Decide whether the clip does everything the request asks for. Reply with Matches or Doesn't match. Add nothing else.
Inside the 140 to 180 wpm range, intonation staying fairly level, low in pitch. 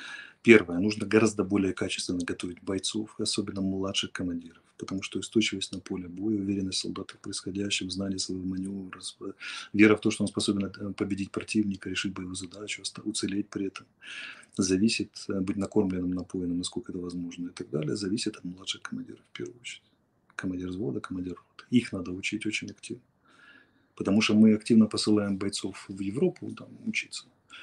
Matches